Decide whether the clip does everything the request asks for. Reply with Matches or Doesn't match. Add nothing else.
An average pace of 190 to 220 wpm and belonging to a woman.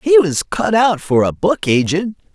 Doesn't match